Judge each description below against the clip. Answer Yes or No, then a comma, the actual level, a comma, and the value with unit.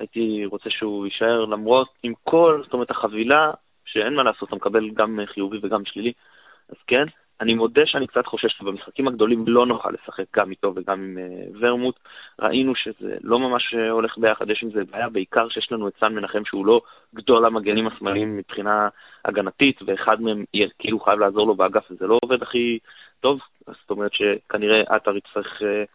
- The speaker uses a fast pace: Yes, fast, 180 wpm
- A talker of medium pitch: No, low, 110 Hz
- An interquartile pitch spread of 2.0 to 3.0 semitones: Yes, narrow, 2.6 semitones